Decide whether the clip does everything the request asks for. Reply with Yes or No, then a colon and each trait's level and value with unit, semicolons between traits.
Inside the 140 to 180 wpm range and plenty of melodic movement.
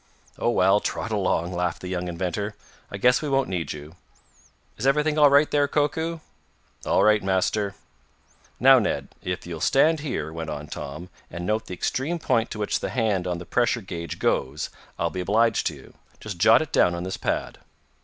No: average, 195 wpm; wide, 6.8 semitones